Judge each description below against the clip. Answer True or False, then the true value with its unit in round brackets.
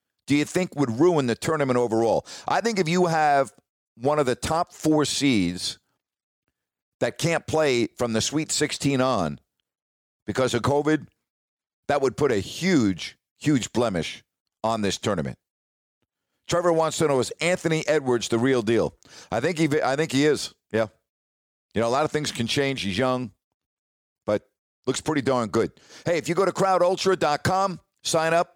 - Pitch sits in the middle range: True (145 Hz)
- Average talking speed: True (170 wpm)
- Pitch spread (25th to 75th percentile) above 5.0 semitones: True (5.4 semitones)